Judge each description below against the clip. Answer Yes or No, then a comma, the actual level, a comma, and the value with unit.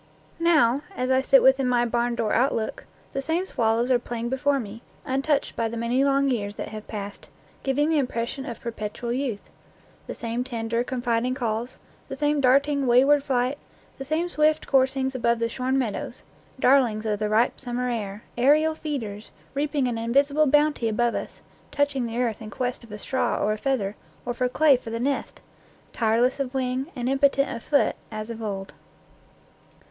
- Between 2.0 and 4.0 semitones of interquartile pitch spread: Yes, average, 3.0 semitones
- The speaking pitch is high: Yes, very high, 250 Hz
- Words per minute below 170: No, average, 180 wpm